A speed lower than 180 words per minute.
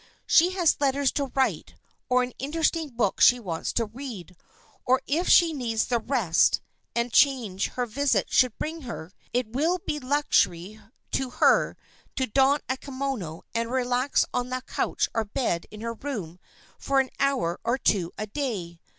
Yes: average, 165 wpm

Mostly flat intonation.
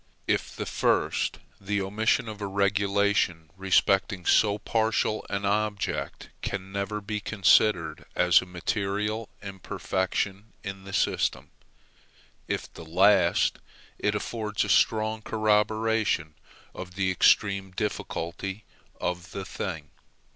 Yes: narrow, 2.1 semitones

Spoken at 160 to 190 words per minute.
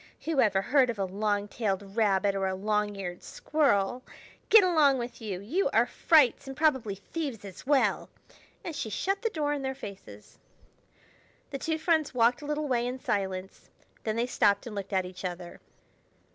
Yes: average, 185 wpm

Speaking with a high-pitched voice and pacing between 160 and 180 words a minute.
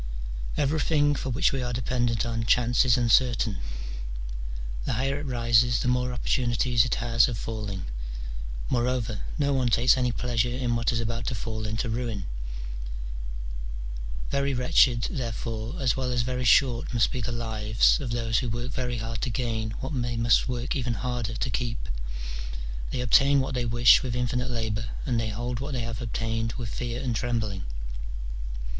No: low, 120 Hz; average, 170 wpm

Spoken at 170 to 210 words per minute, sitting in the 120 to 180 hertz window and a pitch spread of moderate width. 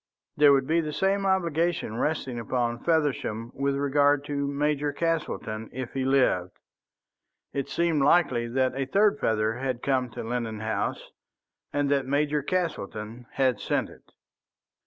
No: average, 145 wpm; medium, 140 Hz; average, 3.9 semitones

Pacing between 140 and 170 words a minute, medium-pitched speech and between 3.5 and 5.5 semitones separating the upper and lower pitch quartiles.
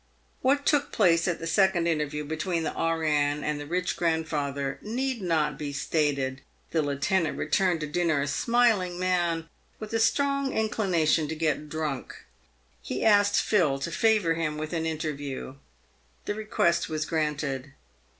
Yes: average, 150 wpm; medium, 165 Hz; average, 4.1 semitones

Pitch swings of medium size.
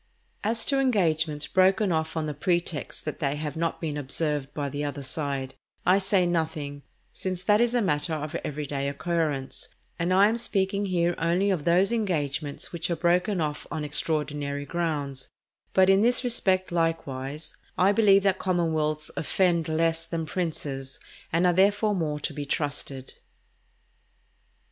Yes: average, 4.1 semitones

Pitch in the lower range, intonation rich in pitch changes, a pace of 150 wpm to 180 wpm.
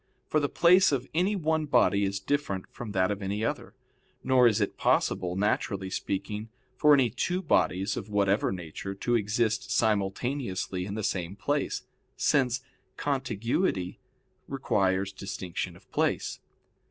No: low, 105 Hz; wide, 5.7 semitones; average, 140 wpm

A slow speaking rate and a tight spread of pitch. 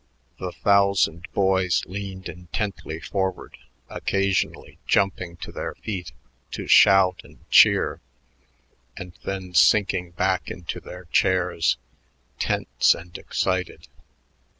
Yes: slow, 105 wpm; narrow, 1.6 semitones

